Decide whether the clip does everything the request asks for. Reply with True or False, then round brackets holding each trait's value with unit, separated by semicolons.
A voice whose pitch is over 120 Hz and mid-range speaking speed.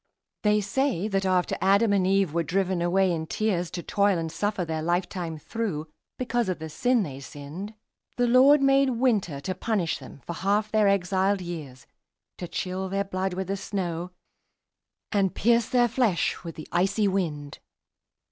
True (190 Hz; 175 wpm)